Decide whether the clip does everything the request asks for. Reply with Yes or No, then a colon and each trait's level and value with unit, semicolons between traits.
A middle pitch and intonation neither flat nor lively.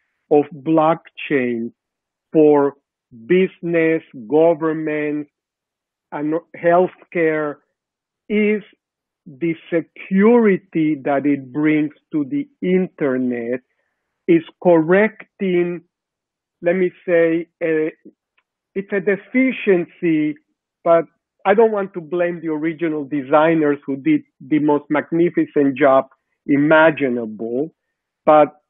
Yes: medium, 160 Hz; average, 3.5 semitones